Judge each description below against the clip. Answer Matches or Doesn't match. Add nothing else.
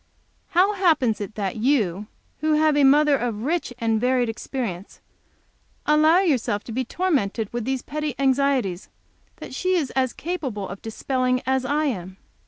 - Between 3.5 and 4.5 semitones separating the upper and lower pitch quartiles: Doesn't match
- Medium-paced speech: Matches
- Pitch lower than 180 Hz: Doesn't match